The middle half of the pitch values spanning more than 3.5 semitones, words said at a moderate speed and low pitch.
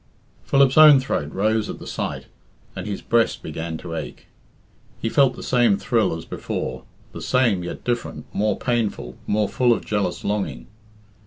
Yes: average, 5.2 semitones; average, 165 wpm; low, 105 Hz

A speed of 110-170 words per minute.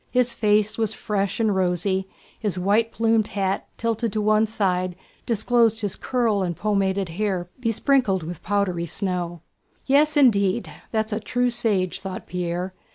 Yes: average, 150 wpm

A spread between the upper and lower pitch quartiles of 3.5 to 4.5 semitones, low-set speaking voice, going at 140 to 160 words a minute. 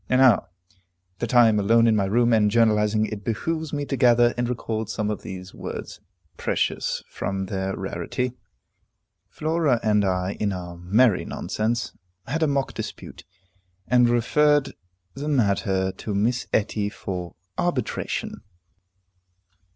Yes: average, 3.8 semitones; low, 110 Hz; average, 145 wpm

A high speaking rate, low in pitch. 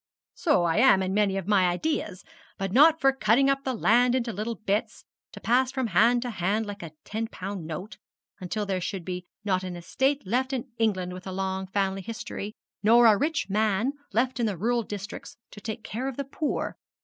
No: fast, 210 wpm; high, 215 Hz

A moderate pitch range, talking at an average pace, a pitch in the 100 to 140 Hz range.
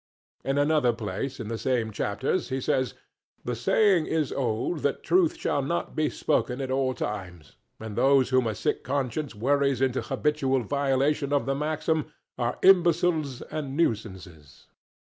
Yes: average, 4.1 semitones; average, 155 wpm; low, 135 Hz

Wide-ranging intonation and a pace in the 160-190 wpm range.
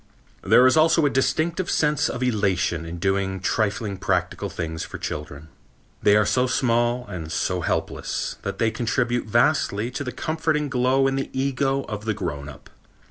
Yes: wide, 5.8 semitones; average, 170 wpm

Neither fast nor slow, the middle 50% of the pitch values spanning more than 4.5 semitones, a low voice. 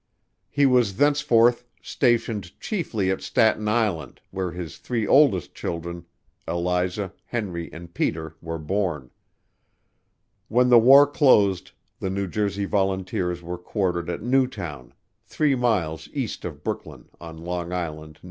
No: slow, 130 wpm; average, 5.2 semitones; very low, 95 Hz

